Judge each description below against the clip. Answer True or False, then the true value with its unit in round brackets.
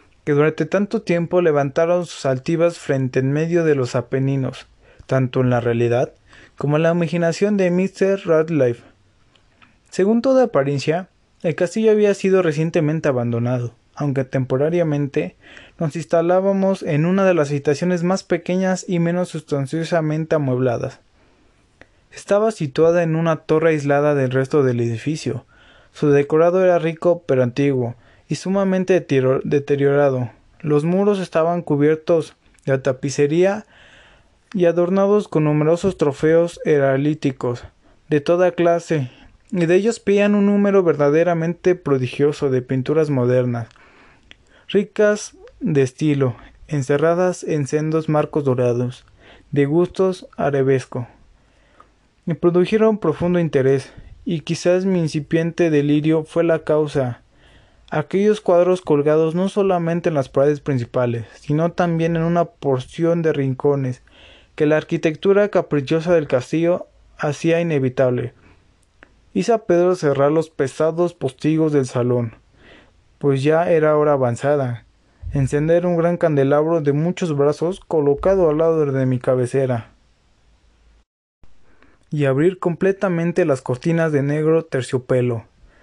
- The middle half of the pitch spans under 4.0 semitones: False (4.4 semitones)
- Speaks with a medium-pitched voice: True (155 Hz)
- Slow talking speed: True (120 wpm)